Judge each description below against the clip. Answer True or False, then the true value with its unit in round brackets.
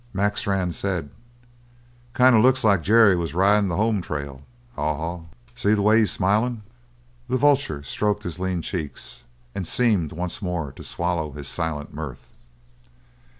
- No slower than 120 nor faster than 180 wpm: True (155 wpm)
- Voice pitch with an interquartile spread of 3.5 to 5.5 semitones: True (4.7 semitones)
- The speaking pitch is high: False (95 Hz)